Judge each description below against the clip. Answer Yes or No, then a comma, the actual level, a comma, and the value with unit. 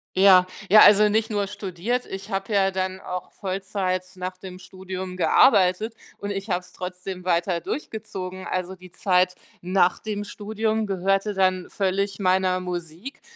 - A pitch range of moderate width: No, narrow, 1.8 semitones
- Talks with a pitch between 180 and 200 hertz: Yes, high, 190 Hz